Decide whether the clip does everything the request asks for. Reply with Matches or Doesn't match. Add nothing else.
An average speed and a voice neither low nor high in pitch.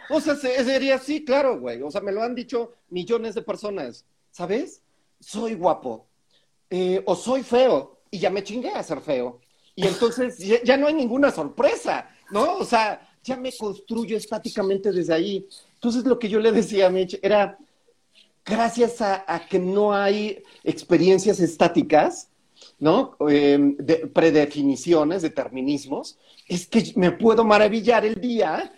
Doesn't match